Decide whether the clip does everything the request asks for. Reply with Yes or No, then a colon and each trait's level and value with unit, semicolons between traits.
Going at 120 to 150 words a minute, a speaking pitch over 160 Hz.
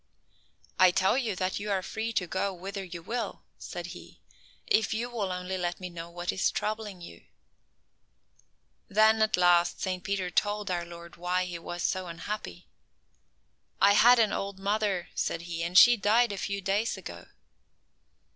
No: average, 170 wpm; high, 190 Hz